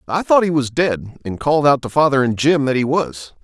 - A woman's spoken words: No, male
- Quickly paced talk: Yes, fast, 260 wpm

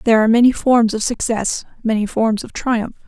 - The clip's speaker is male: No, female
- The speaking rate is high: No, average, 195 wpm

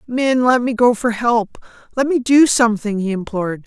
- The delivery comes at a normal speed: Yes, average, 180 wpm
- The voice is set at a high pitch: Yes, high, 230 Hz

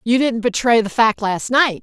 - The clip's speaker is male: No, female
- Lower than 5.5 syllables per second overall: Yes, 4.6 syllables/s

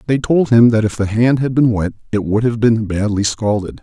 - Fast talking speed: Yes, fast, 250 wpm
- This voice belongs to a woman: No, male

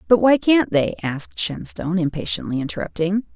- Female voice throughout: Yes, female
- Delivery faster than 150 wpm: No, average, 145 wpm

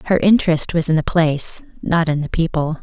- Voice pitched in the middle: Yes, medium, 160 Hz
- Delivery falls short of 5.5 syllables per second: No, 5.7 syllables/s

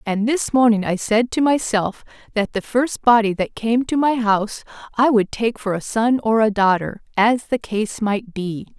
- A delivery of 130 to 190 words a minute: No, average, 200 wpm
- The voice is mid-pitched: No, high, 220 Hz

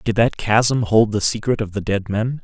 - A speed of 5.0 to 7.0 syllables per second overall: No, 4.7 syllables/s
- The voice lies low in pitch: Yes, low, 110 Hz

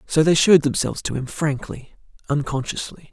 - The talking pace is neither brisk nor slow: Yes, average, 155 wpm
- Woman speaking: No, male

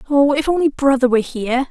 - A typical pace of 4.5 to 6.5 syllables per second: No, 6.7 syllables/s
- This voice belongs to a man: No, female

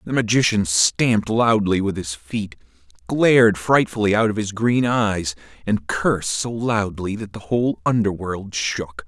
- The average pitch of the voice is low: Yes, low, 105 Hz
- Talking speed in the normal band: Yes, average, 150 wpm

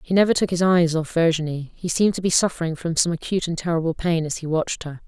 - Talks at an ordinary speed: No, fast, 260 wpm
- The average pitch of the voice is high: No, medium, 165 Hz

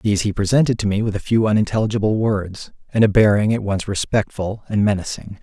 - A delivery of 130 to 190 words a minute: No, average, 200 wpm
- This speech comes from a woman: No, male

